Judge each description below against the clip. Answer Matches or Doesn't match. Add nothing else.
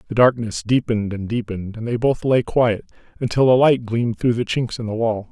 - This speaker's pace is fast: Matches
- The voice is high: Doesn't match